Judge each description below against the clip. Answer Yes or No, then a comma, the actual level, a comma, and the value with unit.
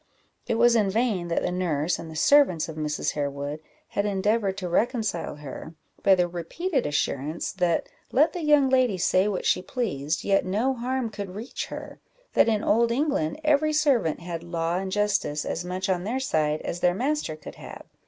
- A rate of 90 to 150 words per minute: No, average, 190 wpm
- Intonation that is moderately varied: No, wide, 6.2 semitones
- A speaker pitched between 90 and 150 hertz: No, high, 190 Hz